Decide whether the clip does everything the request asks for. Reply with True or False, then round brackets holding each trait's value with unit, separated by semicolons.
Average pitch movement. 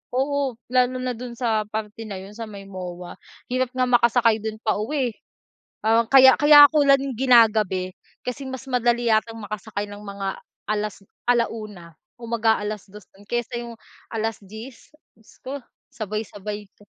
True (3.0 semitones)